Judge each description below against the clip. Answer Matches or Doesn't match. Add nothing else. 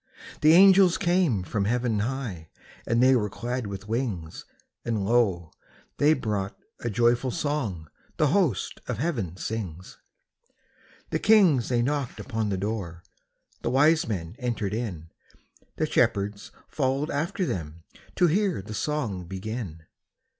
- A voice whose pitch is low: Matches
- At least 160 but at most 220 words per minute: Doesn't match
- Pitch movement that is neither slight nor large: Doesn't match